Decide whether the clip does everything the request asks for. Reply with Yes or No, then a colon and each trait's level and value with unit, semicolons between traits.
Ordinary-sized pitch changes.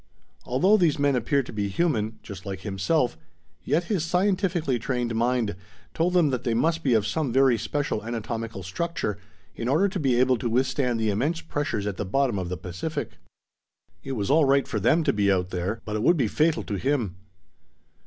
No: wide, 6.4 semitones